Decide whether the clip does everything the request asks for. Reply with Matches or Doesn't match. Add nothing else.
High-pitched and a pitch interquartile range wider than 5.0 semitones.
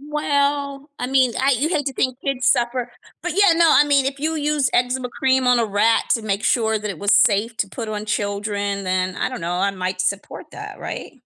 Matches